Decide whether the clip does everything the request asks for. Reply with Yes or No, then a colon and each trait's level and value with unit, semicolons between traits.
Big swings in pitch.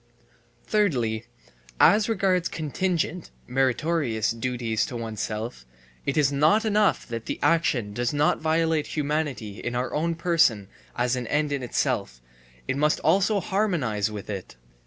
Yes: wide, 6.3 semitones